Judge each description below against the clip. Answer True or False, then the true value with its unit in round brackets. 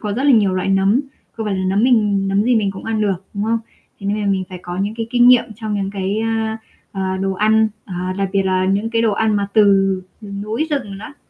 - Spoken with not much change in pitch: True (2.3 semitones)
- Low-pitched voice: False (205 Hz)